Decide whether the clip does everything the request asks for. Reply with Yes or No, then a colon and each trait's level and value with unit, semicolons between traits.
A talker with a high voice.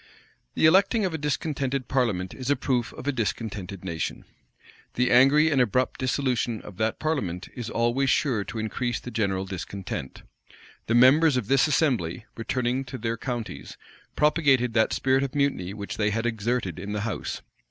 No: low, 120 Hz